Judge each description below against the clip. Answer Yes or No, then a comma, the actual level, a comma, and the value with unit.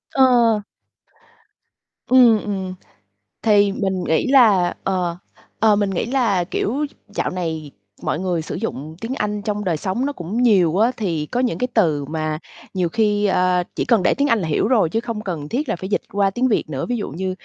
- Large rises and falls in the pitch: No, average, 4.7 semitones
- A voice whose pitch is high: Yes, high, 200 Hz